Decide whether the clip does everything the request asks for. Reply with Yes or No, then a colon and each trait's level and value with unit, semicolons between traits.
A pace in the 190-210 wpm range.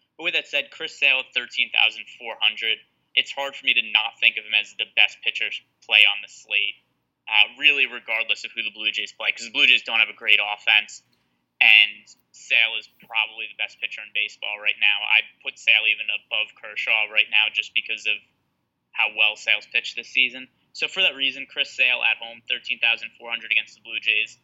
Yes: fast, 205 wpm